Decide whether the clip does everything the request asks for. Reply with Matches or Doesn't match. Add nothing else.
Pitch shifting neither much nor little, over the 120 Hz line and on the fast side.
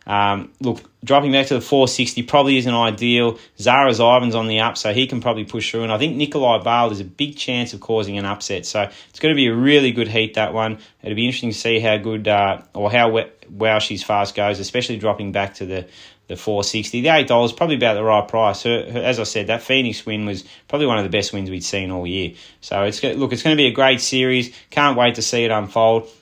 Doesn't match